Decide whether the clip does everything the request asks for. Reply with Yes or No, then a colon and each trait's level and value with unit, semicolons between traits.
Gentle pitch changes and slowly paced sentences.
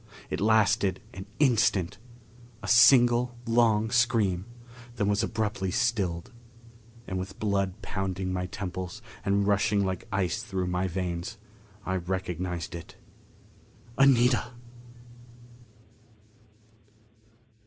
No: average, 3.3 semitones; slow, 100 wpm